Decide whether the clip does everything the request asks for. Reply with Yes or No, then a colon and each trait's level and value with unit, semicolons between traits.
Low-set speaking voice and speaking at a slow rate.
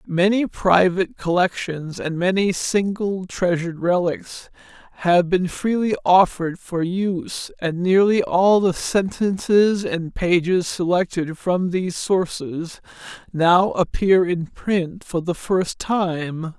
No: medium, 180 Hz; slow, 120 wpm